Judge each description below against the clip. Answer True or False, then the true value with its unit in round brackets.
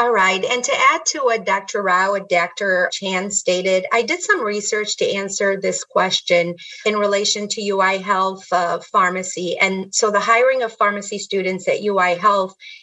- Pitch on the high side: True (200 Hz)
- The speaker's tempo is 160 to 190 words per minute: True (180 wpm)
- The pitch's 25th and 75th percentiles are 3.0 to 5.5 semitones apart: False (2.4 semitones)